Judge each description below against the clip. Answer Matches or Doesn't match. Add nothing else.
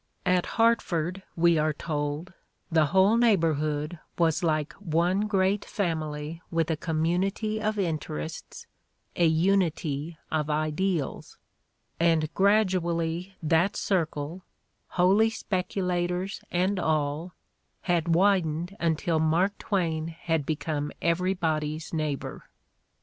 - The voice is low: Doesn't match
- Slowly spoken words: Matches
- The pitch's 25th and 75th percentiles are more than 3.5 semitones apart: Doesn't match